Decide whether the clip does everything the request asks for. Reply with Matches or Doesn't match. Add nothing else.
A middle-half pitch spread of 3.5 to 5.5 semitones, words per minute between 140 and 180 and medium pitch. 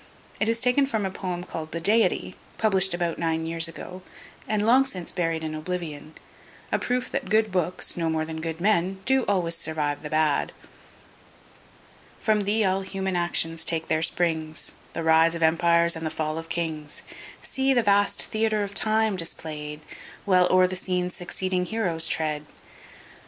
Matches